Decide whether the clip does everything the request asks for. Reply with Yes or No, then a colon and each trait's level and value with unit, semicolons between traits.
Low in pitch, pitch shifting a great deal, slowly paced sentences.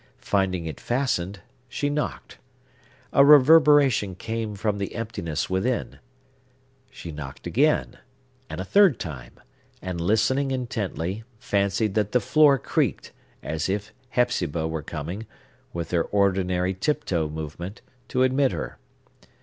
Yes: low, 100 Hz; wide, 6.6 semitones; slow, 125 wpm